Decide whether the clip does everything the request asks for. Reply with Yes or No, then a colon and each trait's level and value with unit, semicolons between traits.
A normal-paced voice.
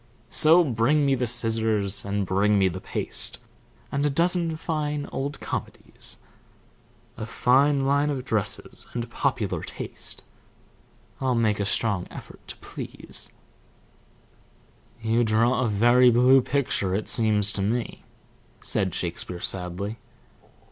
No: slow, 125 wpm